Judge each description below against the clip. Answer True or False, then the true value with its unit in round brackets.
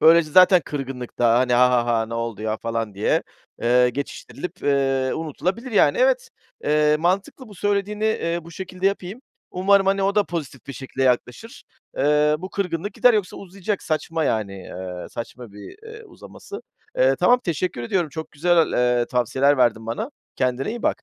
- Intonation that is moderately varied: False (7.8 semitones)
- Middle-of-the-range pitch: True (155 Hz)